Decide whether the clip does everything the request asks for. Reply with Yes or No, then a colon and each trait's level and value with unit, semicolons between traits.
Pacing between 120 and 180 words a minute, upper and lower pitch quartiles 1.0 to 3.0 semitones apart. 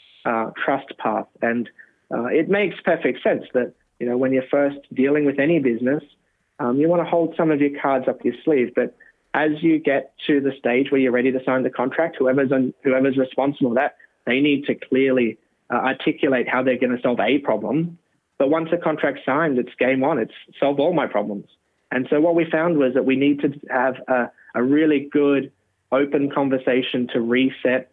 No: fast, 205 wpm; average, 2.7 semitones